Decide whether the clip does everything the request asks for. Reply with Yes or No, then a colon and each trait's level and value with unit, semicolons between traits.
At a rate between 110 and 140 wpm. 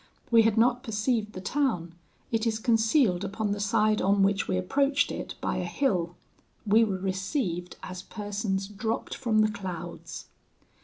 No: average, 160 wpm